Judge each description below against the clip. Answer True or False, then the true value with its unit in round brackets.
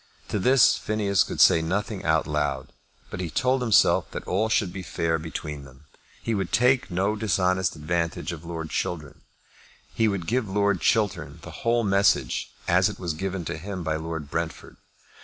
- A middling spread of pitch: True (4.3 semitones)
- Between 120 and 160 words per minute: False (175 wpm)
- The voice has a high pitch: False (90 Hz)